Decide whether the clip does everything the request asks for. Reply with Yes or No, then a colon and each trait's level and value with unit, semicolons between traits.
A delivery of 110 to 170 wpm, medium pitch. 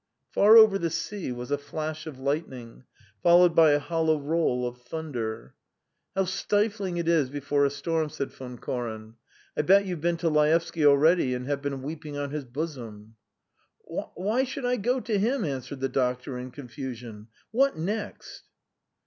Yes: average, 165 wpm; medium, 150 Hz